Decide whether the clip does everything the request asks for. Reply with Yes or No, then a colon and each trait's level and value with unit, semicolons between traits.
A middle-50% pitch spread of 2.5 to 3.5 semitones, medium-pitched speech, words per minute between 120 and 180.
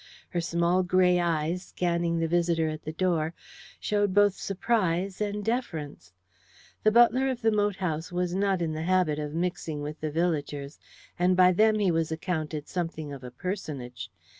Yes: average, 3.2 semitones; medium, 175 Hz; average, 170 wpm